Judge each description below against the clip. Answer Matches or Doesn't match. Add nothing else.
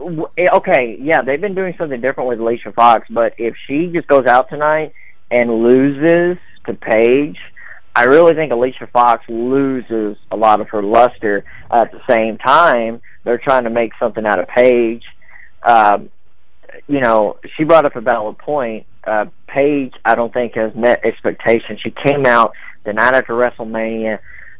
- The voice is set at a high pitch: Doesn't match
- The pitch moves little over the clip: Doesn't match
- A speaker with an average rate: Matches